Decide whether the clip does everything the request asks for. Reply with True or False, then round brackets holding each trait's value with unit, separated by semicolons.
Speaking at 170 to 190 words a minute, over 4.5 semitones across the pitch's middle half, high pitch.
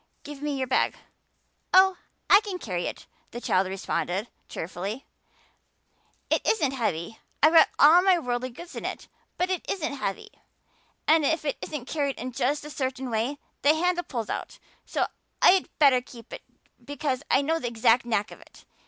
True (175 wpm; 5.2 semitones; 275 Hz)